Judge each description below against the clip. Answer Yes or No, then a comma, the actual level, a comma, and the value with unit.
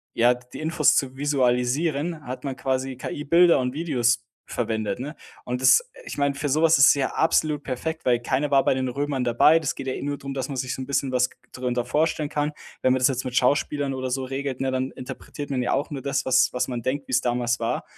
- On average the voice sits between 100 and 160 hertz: Yes, low, 135 Hz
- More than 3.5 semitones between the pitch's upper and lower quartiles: No, narrow, 2.5 semitones